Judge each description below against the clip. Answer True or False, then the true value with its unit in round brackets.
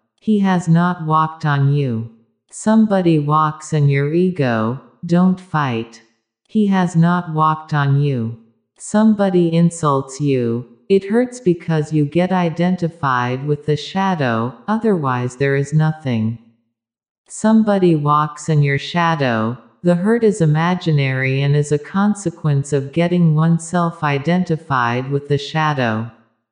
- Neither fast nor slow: False (125 wpm)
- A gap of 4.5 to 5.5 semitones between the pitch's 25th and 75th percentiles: True (5.0 semitones)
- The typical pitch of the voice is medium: True (155 Hz)